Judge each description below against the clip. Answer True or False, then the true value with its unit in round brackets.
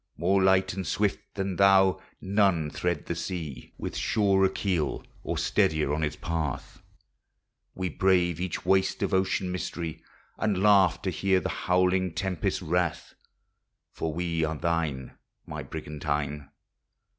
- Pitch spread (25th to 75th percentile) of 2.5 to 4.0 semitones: True (3.3 semitones)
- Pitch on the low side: True (90 Hz)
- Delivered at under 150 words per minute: True (140 wpm)